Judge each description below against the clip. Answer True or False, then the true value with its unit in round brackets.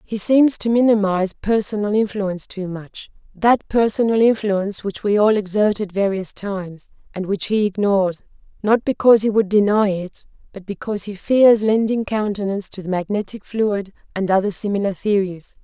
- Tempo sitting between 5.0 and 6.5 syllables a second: True (5.2 syllables/s)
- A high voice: True (205 Hz)